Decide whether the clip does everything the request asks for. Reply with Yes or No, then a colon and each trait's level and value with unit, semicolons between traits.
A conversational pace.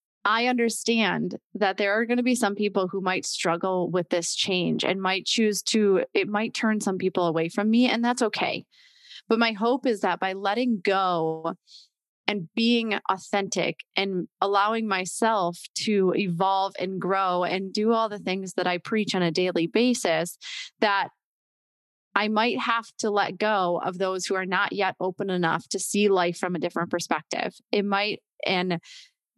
Yes: average, 175 wpm